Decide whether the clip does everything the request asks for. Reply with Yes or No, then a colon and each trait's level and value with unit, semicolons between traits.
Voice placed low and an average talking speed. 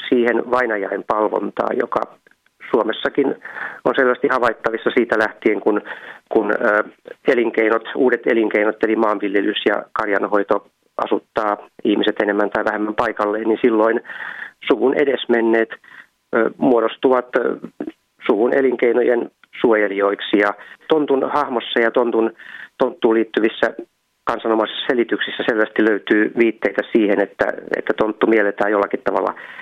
Yes: low, 110 Hz; average, 105 wpm